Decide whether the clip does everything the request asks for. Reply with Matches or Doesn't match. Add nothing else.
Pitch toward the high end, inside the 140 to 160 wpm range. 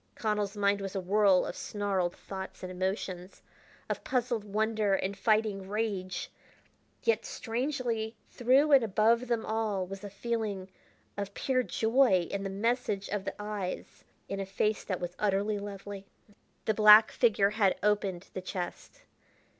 Matches